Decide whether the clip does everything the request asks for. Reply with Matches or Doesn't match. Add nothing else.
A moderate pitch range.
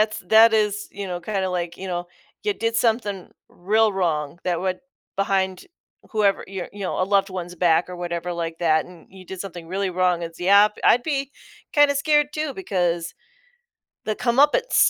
Matches